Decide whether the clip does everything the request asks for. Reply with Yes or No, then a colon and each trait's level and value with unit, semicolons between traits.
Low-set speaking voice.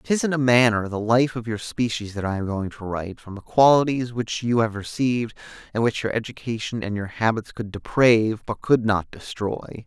Yes: low, 115 Hz